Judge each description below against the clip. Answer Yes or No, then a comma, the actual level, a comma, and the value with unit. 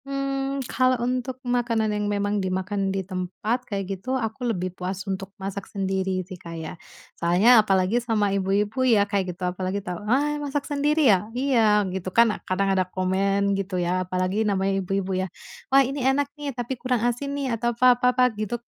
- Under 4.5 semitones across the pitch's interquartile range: No, average, 4.8 semitones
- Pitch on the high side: Yes, high, 205 Hz